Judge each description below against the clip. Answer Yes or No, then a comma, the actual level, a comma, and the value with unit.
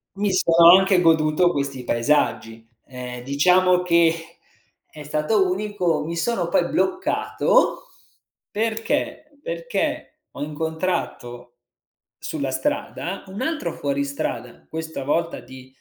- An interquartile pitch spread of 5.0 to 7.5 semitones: Yes, wide, 5.5 semitones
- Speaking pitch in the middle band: Yes, medium, 165 Hz